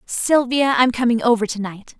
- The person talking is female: Yes, female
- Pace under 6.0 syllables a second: Yes, 4.9 syllables/s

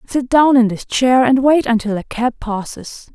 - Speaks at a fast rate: Yes, fast, 210 wpm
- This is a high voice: Yes, high, 245 Hz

